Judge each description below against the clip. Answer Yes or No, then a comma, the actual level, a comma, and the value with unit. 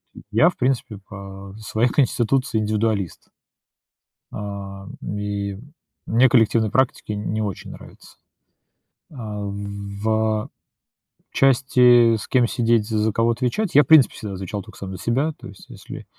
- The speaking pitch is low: Yes, low, 110 Hz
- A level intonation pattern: No, average, 3.2 semitones